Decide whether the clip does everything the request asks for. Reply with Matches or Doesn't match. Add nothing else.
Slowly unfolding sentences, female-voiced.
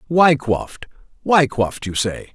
Doesn't match